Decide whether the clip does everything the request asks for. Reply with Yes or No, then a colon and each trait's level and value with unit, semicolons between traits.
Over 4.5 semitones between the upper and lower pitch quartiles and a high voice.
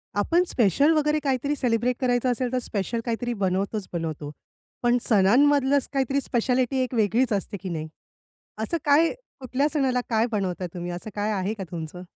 Yes: average, 5.1 semitones; high, 235 Hz